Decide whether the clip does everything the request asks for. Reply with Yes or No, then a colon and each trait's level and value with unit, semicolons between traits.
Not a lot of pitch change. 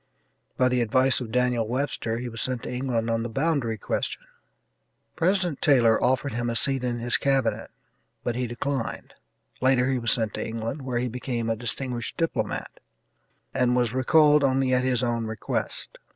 Yes: narrow, 2.3 semitones